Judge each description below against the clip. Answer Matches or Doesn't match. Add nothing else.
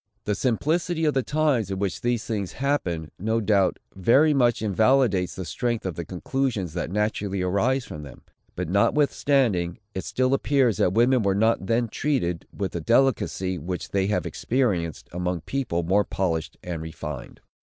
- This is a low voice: Matches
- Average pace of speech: Matches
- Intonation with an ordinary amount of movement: Doesn't match